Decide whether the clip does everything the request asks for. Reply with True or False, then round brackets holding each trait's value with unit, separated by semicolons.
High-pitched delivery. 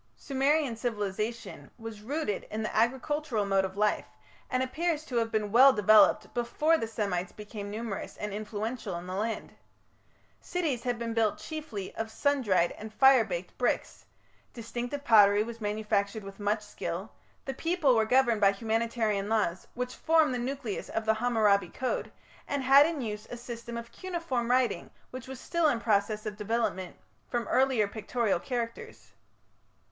True (230 Hz)